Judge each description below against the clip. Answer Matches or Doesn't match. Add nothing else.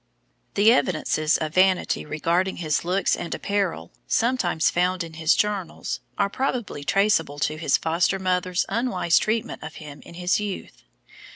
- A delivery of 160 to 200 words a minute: Doesn't match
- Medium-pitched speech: Matches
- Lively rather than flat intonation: Doesn't match